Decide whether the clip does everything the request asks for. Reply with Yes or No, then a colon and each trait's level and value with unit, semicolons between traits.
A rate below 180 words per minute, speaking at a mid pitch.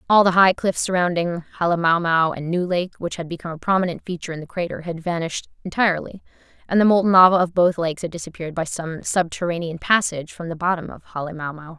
No: average, 200 wpm; medium, 170 Hz